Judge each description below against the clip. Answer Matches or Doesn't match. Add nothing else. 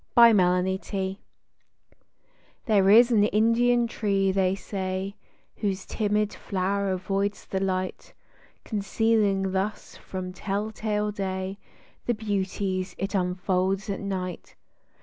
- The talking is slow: Matches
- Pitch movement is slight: Matches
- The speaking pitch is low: Doesn't match